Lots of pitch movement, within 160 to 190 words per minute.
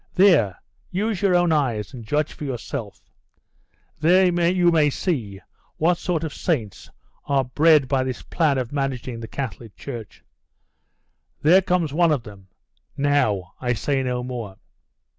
No: wide, 5.7 semitones; average, 145 wpm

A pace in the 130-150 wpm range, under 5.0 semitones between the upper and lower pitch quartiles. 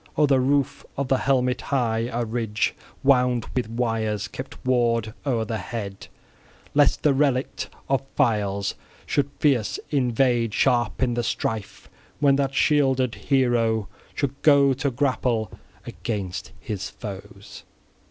Yes: slow, 135 wpm; average, 3.5 semitones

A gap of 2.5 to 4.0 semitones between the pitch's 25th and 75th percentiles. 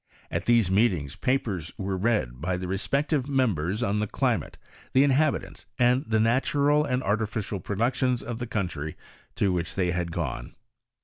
No: wide, 5.6 semitones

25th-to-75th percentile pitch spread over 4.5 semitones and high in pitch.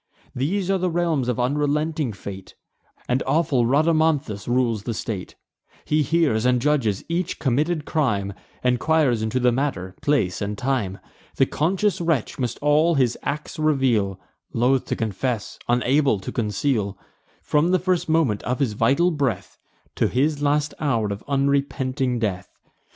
No: average, 5.2 semitones; low, 135 Hz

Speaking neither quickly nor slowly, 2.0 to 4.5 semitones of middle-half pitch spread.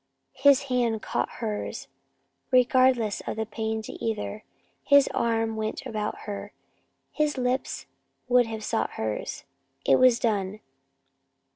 No: slow, 125 wpm; average, 2.8 semitones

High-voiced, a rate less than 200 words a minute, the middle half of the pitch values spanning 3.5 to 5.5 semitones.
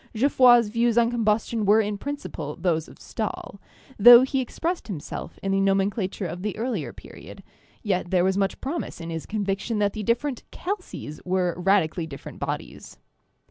Yes: high, 205 Hz; average, 170 wpm; average, 4.3 semitones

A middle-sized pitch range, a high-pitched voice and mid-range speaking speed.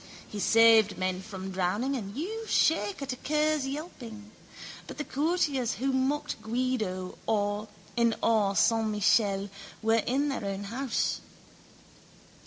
No: average, 5.0 semitones; high, 230 Hz; slow, 130 wpm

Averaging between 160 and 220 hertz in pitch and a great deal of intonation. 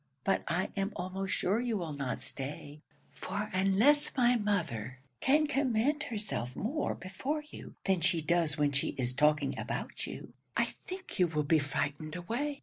Yes: medium, 185 Hz; wide, 7.6 semitones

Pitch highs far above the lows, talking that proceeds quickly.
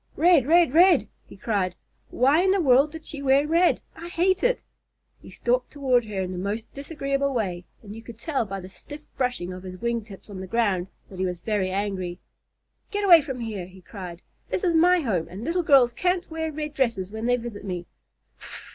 Yes: wide, 8.0 semitones; fast, 210 wpm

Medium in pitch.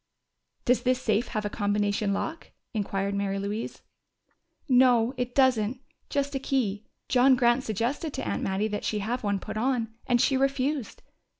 No: high, 235 Hz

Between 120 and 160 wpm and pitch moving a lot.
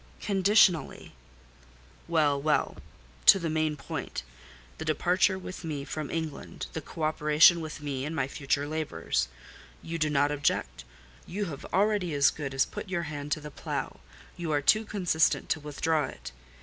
No: average, 150 wpm; average, 3.0 semitones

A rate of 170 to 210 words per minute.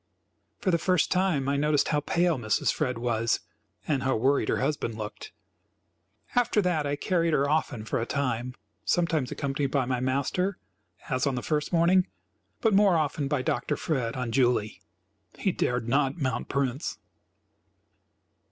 No: average, 160 wpm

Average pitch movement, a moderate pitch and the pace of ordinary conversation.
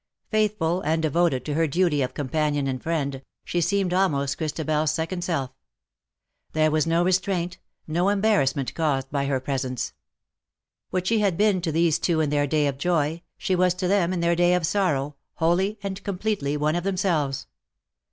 Yes: average, 4.0 semitones; medium, 165 Hz; average, 180 wpm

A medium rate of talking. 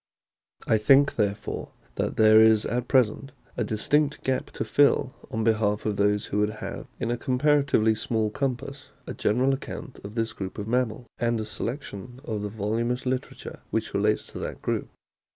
Yes: average, 175 wpm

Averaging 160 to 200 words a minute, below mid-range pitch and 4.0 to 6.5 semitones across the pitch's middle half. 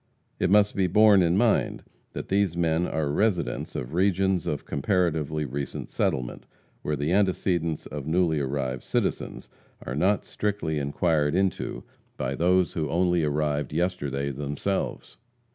No: average, 140 wpm; very low, 80 Hz; average, 4.3 semitones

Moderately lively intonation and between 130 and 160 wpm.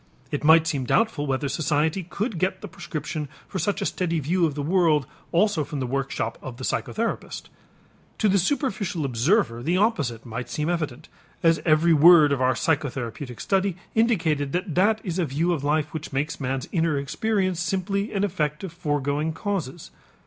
No: average, 4.7 semitones; average, 180 wpm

